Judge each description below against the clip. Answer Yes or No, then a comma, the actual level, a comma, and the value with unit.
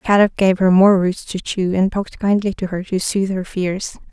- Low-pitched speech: No, high, 190 Hz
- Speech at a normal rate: No, fast, 235 wpm